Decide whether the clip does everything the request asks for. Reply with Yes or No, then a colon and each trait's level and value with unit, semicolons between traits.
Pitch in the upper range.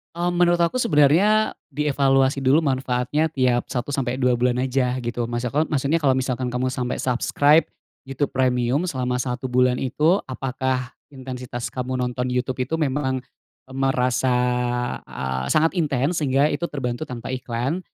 No: low, 130 Hz